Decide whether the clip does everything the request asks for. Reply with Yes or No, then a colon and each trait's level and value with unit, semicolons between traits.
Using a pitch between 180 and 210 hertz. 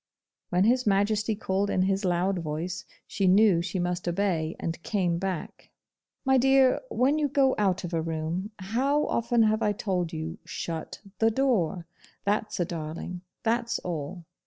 Yes: high, 190 Hz